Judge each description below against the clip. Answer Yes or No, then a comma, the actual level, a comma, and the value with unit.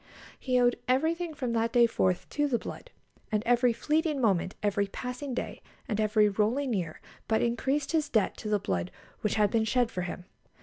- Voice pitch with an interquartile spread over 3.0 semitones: Yes, average, 4.0 semitones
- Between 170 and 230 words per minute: Yes, average, 190 wpm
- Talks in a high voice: Yes, high, 235 Hz